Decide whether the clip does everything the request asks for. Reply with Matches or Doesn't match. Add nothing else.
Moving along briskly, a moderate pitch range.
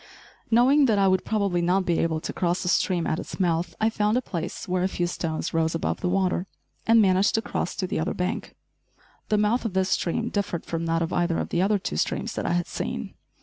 Matches